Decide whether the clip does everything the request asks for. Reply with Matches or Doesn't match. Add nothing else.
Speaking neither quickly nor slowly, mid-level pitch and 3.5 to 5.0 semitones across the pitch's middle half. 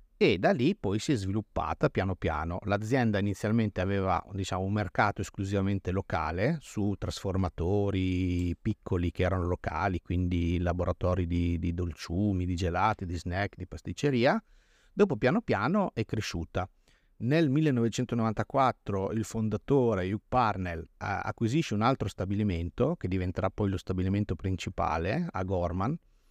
Doesn't match